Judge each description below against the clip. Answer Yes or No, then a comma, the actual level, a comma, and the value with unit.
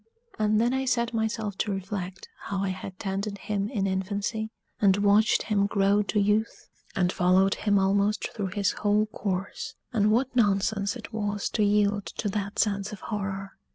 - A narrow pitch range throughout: Yes, narrow, 1.6 semitones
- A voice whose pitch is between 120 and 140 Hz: No, high, 205 Hz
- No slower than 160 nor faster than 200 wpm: Yes, average, 175 wpm